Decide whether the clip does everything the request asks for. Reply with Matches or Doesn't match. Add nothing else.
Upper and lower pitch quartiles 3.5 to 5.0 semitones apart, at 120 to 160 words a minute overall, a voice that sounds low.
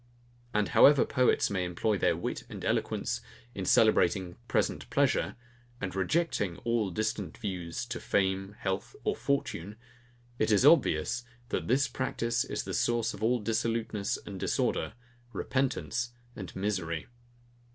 Matches